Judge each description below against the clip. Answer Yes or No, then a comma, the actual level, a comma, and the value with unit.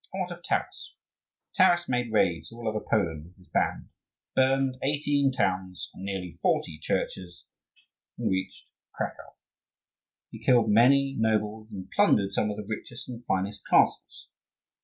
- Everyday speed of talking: Yes, average, 145 wpm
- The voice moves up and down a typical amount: No, wide, 5.8 semitones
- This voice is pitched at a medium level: No, low, 110 Hz